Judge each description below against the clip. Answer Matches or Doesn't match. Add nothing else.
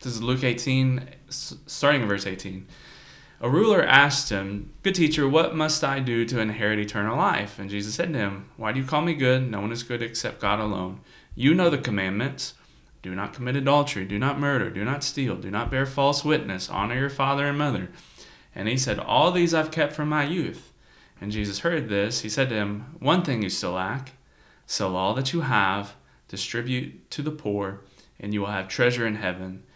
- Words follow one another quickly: Matches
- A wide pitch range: Matches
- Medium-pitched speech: Doesn't match